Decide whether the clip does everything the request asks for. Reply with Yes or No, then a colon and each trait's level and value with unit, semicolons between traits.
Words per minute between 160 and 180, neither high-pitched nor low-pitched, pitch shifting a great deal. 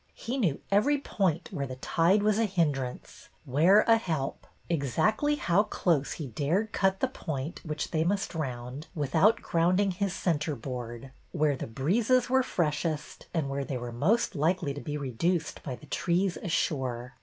Yes: average, 165 wpm; medium, 165 Hz; wide, 6.0 semitones